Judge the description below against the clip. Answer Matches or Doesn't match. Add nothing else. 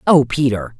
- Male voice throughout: Doesn't match